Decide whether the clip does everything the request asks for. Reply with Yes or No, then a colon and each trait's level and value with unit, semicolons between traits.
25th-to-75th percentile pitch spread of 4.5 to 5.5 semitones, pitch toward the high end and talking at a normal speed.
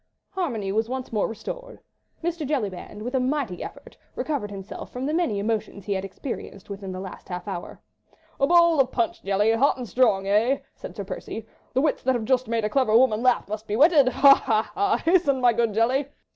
No: average, 5.0 semitones; high, 235 Hz; fast, 210 wpm